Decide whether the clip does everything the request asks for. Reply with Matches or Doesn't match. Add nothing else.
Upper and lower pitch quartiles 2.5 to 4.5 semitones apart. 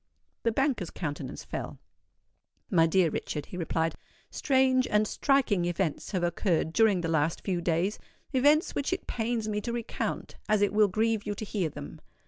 Doesn't match